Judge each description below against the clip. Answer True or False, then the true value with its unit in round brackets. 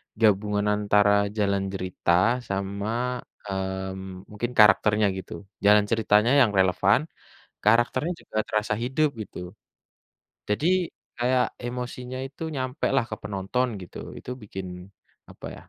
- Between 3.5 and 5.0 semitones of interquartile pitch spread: True (4.1 semitones)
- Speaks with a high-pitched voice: False (105 Hz)